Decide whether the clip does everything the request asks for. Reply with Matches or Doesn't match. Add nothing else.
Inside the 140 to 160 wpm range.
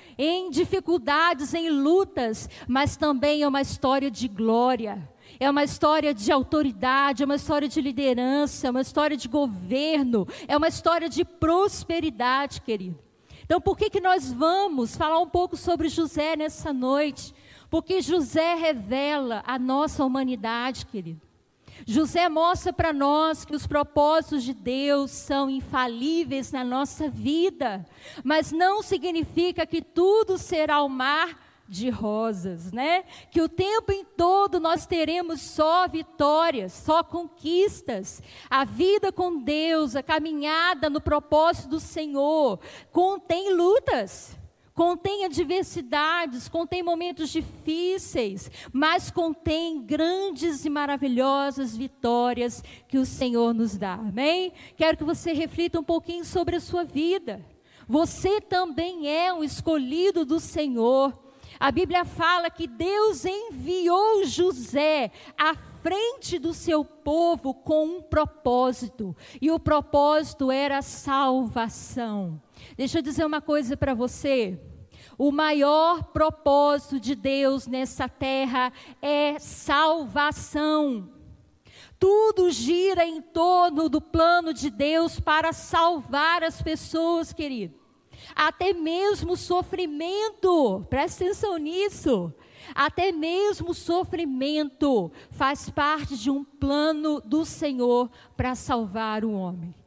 Doesn't match